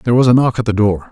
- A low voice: Yes, low, 115 Hz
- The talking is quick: Yes, fast, 375 wpm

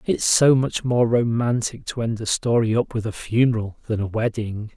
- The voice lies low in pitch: Yes, low, 115 Hz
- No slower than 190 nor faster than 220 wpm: Yes, average, 200 wpm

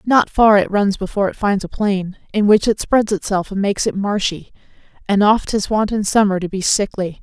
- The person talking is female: Yes, female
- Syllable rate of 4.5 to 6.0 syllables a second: Yes, 5.3 syllables/s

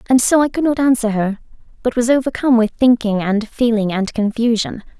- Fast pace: No, average, 190 wpm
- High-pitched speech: Yes, high, 235 Hz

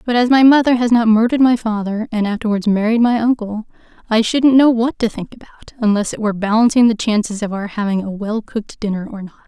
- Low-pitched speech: No, high, 220 Hz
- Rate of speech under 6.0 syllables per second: No, 6.2 syllables/s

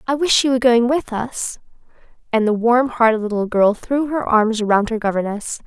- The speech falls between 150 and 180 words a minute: No, average, 200 wpm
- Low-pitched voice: No, high, 235 Hz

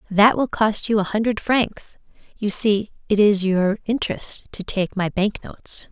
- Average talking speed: Yes, average, 185 wpm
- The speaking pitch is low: No, high, 205 Hz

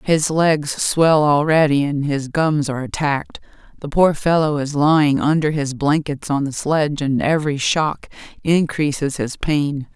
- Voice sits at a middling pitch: Yes, medium, 150 Hz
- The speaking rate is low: No, average, 155 wpm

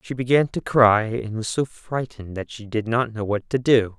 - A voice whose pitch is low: Yes, low, 115 Hz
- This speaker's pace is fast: Yes, fast, 240 wpm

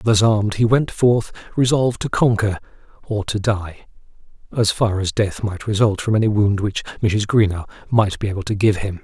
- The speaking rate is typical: Yes, average, 185 wpm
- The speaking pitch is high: No, low, 105 Hz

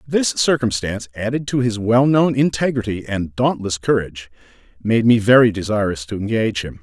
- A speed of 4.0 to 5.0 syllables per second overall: No, 5.4 syllables/s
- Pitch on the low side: Yes, low, 110 Hz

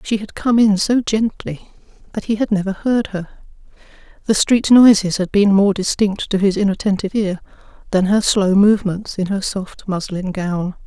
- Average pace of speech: Yes, average, 175 wpm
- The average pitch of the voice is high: Yes, high, 200 Hz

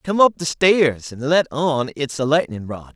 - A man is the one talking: Yes, male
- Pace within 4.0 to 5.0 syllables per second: Yes, 4.3 syllables/s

